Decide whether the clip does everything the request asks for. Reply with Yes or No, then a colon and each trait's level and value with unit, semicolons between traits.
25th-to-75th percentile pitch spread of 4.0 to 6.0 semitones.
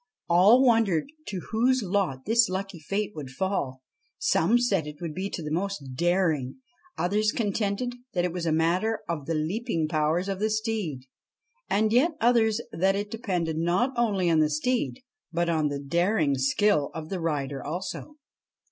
Yes: wide, 5.4 semitones